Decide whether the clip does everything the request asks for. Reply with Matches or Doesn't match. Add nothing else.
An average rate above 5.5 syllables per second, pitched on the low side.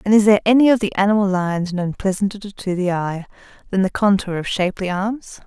Doesn't match